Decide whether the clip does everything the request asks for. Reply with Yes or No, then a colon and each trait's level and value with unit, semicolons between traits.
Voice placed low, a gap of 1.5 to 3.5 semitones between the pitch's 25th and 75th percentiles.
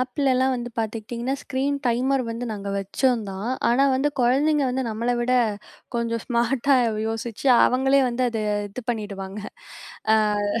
No: high, 240 Hz; average, 2.7 semitones